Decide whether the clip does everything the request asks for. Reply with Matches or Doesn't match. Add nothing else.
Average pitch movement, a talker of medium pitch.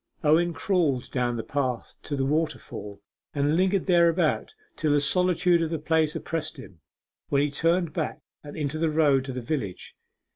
Matches